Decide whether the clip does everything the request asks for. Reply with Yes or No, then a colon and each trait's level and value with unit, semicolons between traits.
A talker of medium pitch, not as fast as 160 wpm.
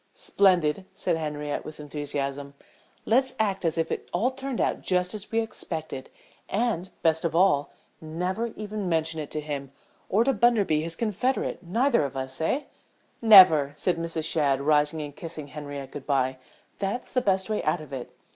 No: medium, 165 Hz; average, 170 wpm